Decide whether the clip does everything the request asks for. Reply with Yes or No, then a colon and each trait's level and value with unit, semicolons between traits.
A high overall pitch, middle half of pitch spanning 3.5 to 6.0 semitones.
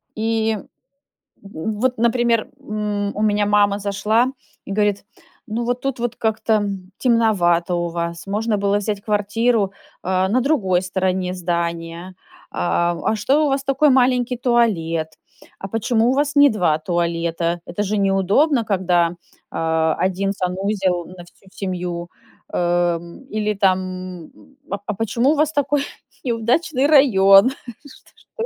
Yes: high, 205 Hz; average, 4.5 semitones